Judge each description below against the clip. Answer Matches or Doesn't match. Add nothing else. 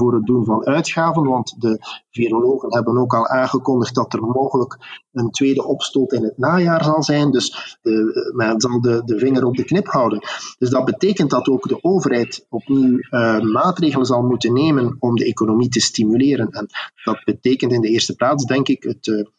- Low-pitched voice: Matches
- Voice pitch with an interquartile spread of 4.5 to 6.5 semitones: Doesn't match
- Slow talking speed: Doesn't match